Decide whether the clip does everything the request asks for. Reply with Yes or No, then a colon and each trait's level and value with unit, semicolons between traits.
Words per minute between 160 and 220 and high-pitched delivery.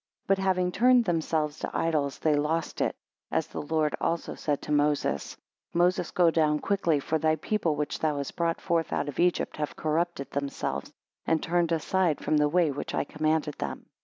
No: average, 190 wpm; medium, 160 Hz